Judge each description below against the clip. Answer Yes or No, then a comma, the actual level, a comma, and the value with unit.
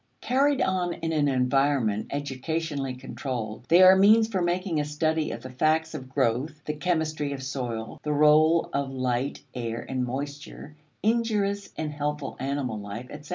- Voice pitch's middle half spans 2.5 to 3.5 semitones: No, average, 4.0 semitones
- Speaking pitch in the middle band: Yes, medium, 145 Hz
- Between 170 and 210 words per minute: No, average, 160 wpm